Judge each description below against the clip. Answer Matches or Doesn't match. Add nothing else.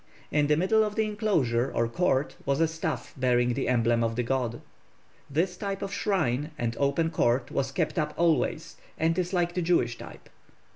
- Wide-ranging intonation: Matches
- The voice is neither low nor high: Matches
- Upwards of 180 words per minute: Matches